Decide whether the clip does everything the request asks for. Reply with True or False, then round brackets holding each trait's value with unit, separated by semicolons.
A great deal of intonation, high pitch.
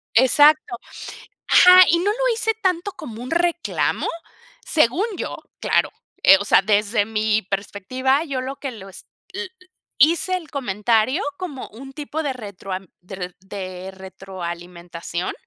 True (8.7 semitones; 240 Hz)